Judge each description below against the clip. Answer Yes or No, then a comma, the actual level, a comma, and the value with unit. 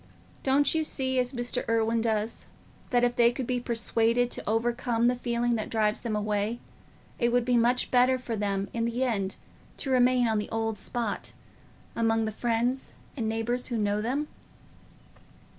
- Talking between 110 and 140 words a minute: No, average, 175 wpm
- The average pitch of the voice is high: Yes, high, 235 Hz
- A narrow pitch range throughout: Yes, narrow, 1.8 semitones